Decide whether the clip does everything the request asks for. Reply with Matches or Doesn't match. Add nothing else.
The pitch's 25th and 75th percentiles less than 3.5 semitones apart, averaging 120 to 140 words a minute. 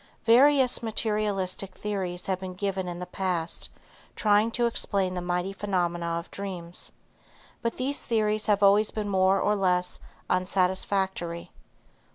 Matches